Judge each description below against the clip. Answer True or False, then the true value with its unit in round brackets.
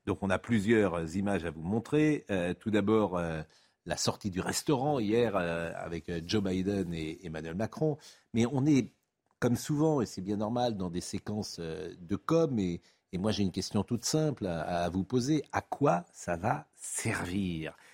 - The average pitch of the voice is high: False (100 Hz)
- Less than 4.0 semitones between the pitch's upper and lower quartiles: False (5.3 semitones)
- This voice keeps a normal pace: True (190 wpm)